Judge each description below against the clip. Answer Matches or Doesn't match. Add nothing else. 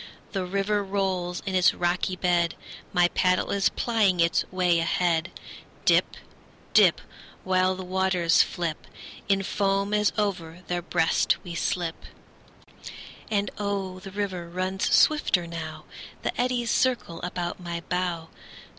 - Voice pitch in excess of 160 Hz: Matches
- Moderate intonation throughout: Doesn't match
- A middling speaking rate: Doesn't match